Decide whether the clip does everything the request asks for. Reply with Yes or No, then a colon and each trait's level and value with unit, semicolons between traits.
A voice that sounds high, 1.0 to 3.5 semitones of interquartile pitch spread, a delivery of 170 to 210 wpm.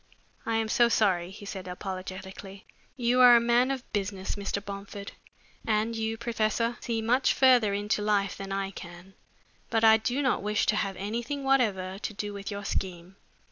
Yes: high, 210 Hz; average, 3.1 semitones; average, 180 wpm